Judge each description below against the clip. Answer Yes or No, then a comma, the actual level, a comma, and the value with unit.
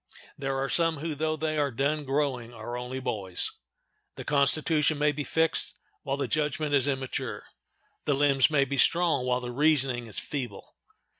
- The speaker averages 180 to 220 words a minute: No, average, 170 wpm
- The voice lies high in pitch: No, medium, 140 Hz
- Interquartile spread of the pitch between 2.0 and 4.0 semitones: Yes, average, 2.9 semitones